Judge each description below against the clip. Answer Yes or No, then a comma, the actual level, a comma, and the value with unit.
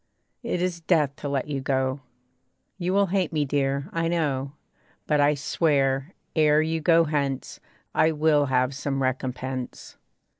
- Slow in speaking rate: No, average, 150 wpm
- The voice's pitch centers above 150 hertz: No, medium, 145 Hz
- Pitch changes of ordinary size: Yes, average, 3.1 semitones